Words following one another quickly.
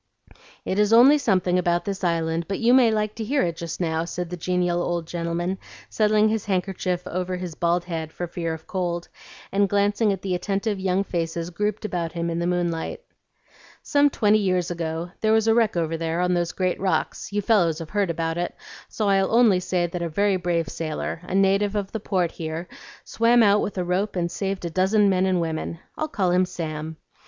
Yes: fast, 210 wpm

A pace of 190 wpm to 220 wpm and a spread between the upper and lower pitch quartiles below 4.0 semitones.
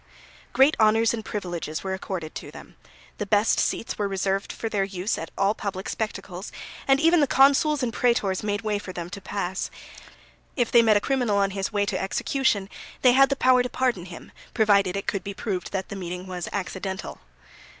Yes: average, 200 wpm; average, 3.6 semitones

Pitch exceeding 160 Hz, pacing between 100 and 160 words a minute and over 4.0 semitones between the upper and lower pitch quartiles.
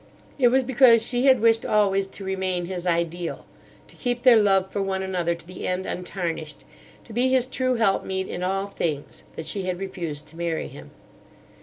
No: high, 190 Hz; average, 190 wpm; average, 4.6 semitones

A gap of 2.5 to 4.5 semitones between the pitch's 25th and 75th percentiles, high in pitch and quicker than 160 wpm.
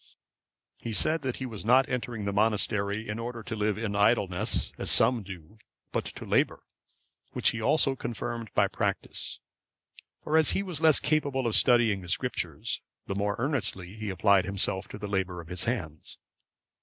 No: average, 3.7 semitones; low, 110 Hz; average, 175 wpm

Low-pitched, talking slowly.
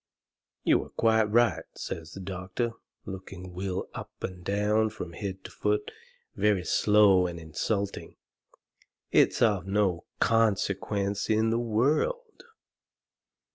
Yes: low, 100 Hz; slow, 120 wpm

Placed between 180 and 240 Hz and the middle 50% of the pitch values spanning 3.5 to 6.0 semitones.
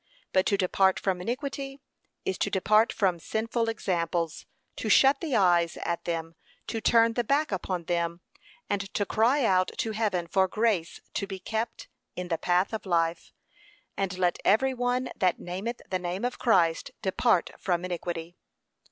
Yes: high, 190 Hz; average, 4.5 semitones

